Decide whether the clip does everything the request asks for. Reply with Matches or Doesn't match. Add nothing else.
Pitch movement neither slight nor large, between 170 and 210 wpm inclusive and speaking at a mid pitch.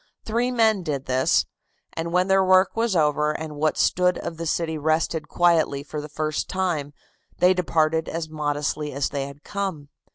Matches